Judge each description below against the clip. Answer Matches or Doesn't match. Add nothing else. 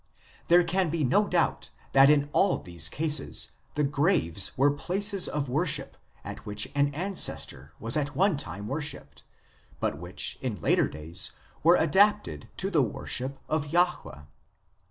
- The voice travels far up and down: Matches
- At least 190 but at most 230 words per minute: Doesn't match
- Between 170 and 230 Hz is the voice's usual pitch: Doesn't match